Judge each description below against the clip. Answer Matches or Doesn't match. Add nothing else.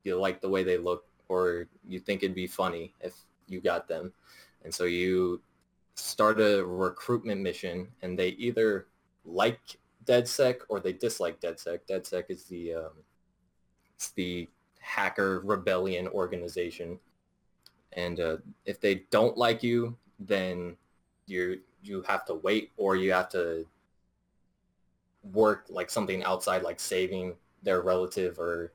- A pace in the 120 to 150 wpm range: Matches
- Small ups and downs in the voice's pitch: Matches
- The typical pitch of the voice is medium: Doesn't match